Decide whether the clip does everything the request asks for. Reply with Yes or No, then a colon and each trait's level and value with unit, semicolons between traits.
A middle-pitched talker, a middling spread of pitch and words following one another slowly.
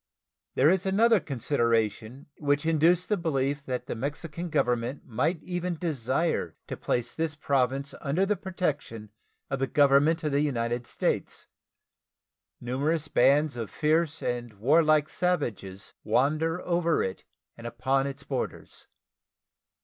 Yes: medium, 145 Hz; average, 4.8 semitones; slow, 130 wpm